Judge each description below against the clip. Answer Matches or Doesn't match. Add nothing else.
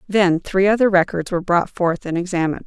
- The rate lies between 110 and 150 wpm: Doesn't match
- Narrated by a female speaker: Matches